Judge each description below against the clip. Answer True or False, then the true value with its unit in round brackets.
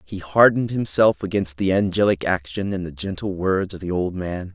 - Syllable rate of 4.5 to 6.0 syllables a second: True (5.2 syllables/s)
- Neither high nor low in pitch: False (95 Hz)